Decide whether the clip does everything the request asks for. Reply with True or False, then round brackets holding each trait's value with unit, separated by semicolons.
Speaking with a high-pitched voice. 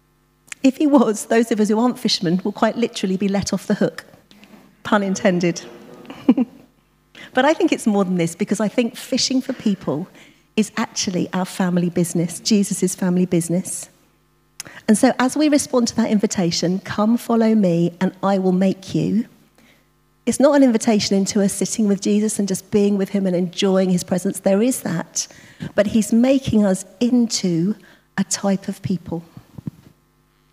True (205 Hz)